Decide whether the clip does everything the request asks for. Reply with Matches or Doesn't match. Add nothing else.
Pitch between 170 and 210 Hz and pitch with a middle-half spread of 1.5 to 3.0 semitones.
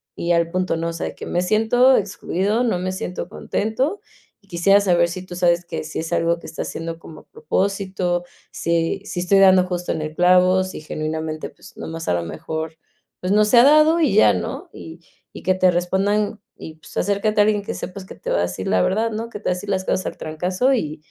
Doesn't match